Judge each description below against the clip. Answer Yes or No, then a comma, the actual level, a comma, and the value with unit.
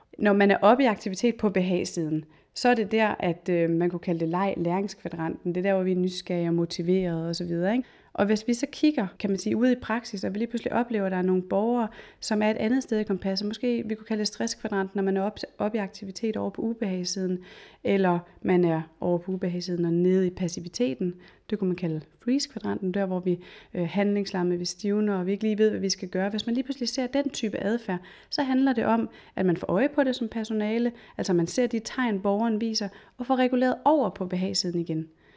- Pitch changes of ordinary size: Yes, average, 4.1 semitones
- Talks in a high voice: Yes, high, 200 Hz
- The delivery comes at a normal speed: No, fast, 235 wpm